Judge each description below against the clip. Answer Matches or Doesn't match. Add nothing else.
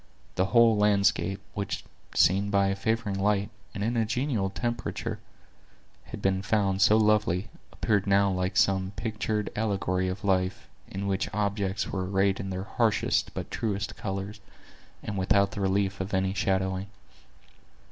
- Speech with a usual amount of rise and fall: Doesn't match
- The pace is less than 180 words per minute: Matches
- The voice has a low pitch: Matches